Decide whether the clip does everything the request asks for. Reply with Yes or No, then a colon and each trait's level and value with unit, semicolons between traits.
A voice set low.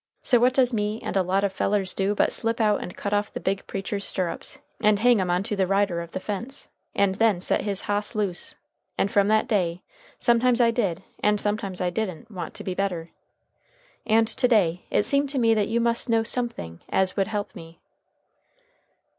No: high, 205 Hz